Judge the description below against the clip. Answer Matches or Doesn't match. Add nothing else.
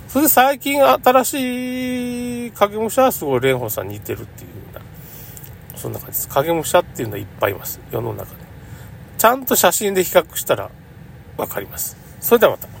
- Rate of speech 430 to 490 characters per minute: Doesn't match